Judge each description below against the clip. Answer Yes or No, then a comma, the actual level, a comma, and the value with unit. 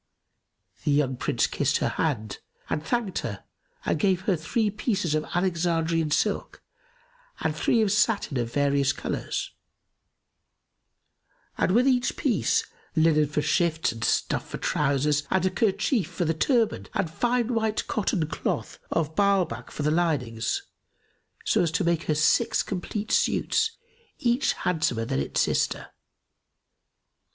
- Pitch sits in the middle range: Yes, medium, 170 Hz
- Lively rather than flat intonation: Yes, wide, 5.7 semitones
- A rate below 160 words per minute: Yes, average, 140 wpm